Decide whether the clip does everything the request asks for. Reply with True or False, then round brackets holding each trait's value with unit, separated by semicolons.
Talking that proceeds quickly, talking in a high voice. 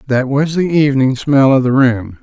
False (215 wpm; 135 Hz)